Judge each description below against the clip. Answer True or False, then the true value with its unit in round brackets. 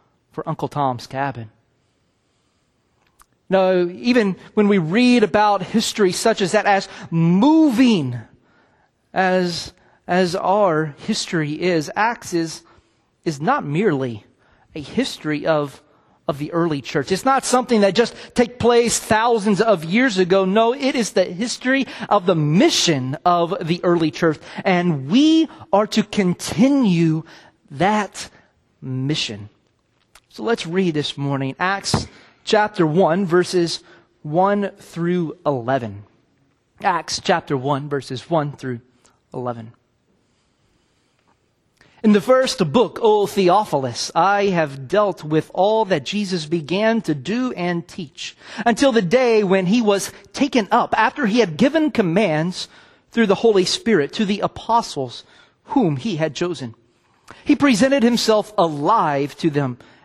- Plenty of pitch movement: True (6.2 semitones)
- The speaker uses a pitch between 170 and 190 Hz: True (185 Hz)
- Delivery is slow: True (130 wpm)